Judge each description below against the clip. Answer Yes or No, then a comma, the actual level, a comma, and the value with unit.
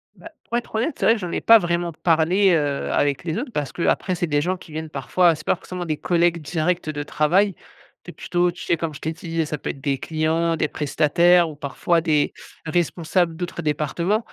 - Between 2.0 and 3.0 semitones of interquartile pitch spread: Yes, narrow, 2.6 semitones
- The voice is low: No, medium, 170 Hz